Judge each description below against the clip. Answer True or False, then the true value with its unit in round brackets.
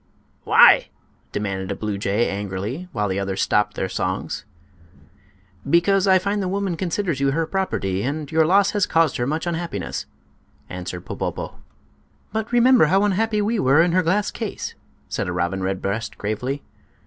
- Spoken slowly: False (160 wpm)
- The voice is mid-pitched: True (155 Hz)